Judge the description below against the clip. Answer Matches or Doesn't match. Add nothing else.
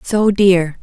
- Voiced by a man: Doesn't match